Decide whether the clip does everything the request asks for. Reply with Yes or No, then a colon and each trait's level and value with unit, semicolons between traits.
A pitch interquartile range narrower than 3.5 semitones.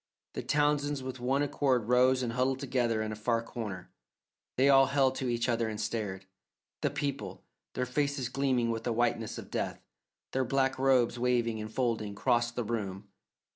Yes: average, 2.8 semitones